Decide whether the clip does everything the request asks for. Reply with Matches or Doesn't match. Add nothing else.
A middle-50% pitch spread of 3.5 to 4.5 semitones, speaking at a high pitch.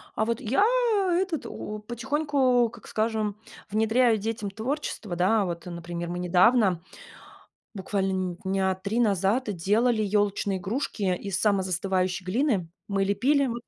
Matches